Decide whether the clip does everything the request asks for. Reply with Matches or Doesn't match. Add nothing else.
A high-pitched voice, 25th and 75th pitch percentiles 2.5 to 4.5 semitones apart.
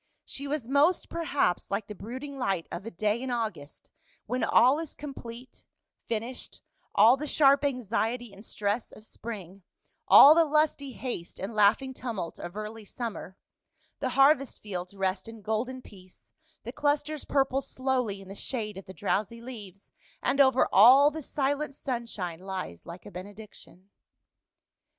Doesn't match